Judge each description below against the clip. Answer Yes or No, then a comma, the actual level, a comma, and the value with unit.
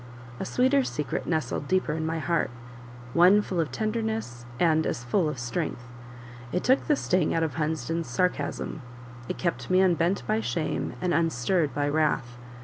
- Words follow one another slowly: No, average, 165 wpm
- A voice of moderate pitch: Yes, medium, 165 Hz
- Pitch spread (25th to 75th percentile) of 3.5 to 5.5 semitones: Yes, average, 4.2 semitones